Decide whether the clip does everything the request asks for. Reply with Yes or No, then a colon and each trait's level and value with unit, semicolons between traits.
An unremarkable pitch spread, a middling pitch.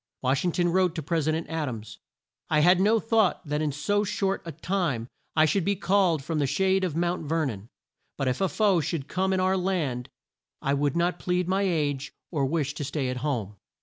Yes: average, 4.7 semitones; medium, 165 Hz